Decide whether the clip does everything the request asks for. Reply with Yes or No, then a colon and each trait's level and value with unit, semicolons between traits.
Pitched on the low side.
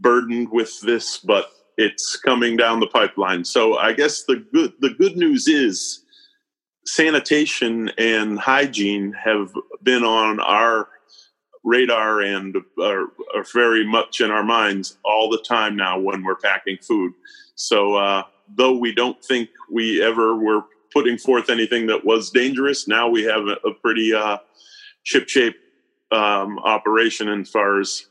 Yes: low, 115 Hz